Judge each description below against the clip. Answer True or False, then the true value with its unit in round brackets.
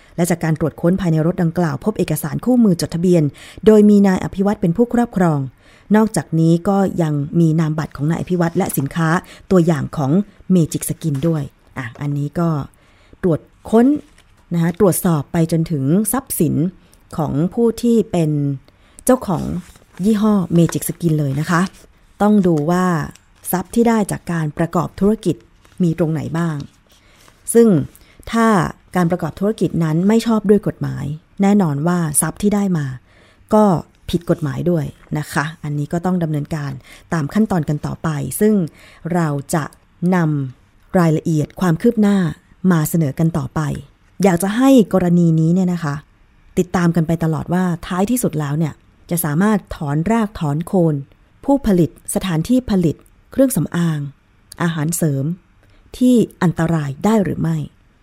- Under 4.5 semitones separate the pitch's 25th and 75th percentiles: True (3.9 semitones)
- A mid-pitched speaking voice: True (170 Hz)